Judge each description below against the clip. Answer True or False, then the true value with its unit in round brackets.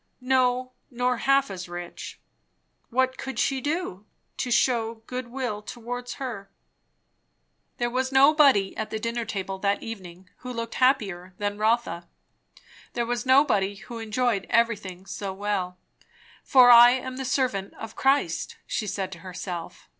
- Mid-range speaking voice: False (230 Hz)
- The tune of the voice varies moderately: True (4.4 semitones)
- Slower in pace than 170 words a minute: True (145 wpm)